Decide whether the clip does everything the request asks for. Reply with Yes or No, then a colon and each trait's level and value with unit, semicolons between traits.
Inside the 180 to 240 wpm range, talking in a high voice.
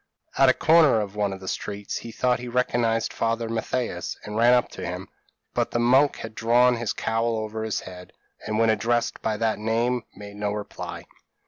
No: average, 200 wpm; low, 115 Hz